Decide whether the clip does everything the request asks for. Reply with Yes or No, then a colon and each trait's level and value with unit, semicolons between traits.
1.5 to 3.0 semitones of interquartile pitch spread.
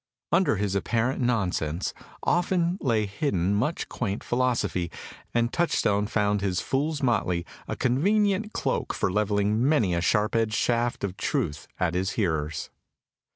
No: average, 5.2 semitones